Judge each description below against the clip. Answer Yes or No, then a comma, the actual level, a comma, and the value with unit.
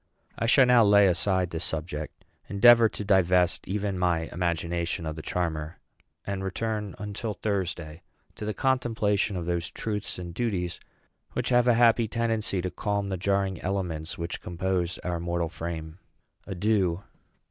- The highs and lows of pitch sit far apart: No, average, 3.5 semitones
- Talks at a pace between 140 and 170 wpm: Yes, average, 150 wpm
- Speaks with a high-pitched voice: No, very low, 95 Hz